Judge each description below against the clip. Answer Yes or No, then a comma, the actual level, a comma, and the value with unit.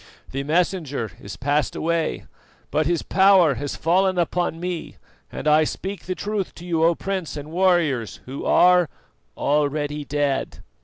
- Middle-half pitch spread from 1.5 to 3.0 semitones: No, average, 3.7 semitones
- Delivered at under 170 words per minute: Yes, average, 150 wpm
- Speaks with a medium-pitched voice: Yes, medium, 165 Hz